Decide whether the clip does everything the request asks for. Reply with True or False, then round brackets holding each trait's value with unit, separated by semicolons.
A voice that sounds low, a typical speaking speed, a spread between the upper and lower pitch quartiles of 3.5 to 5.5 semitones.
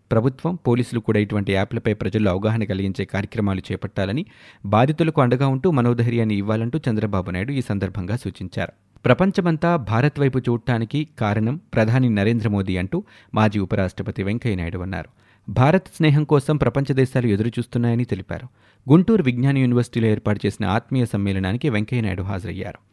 False (115 Hz; 130 wpm; 4.4 semitones)